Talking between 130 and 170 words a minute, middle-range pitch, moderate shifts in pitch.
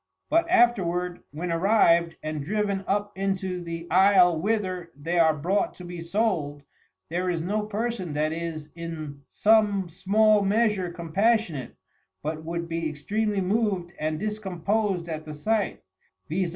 Yes: average, 140 wpm; medium, 180 Hz; average, 3.8 semitones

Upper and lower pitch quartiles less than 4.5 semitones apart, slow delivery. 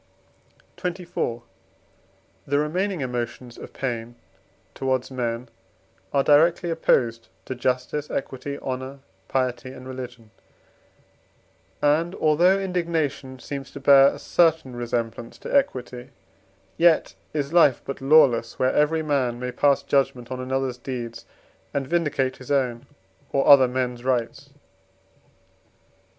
Yes: average, 3.2 semitones; slow, 115 wpm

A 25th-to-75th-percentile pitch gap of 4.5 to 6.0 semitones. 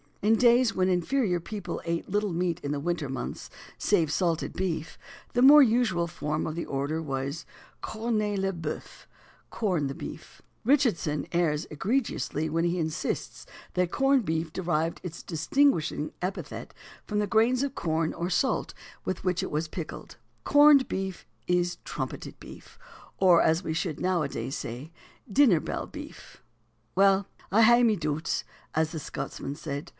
Yes: average, 5.0 semitones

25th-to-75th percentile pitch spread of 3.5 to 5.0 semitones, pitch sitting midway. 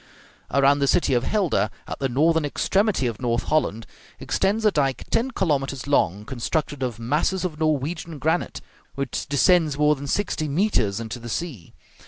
Yes: average, 4.7 semitones; medium, 145 Hz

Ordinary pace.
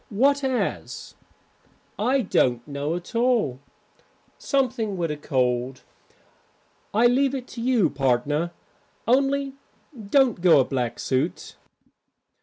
No: slow, 110 wpm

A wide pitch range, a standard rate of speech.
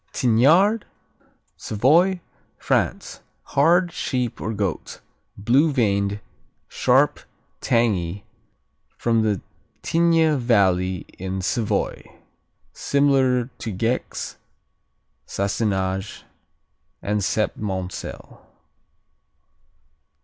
No: wide, 6.0 semitones; slow, 65 wpm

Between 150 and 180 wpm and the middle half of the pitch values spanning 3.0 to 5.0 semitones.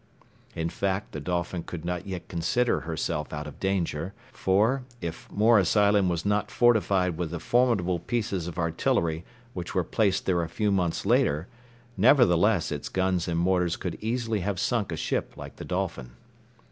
Yes: average, 170 wpm; average, 3.5 semitones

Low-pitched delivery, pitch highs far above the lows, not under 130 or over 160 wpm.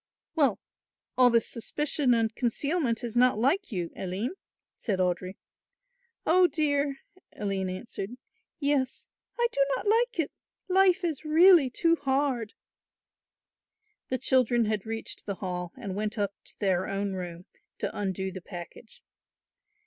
No: high, 240 Hz; wide, 6.7 semitones; slow, 135 wpm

